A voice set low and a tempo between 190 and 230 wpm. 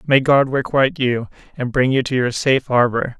Yes: low, 130 Hz; fast, 205 wpm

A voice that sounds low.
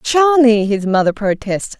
No: high, 230 Hz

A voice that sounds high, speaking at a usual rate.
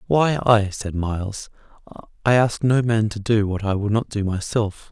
No: low, 110 Hz; average, 195 wpm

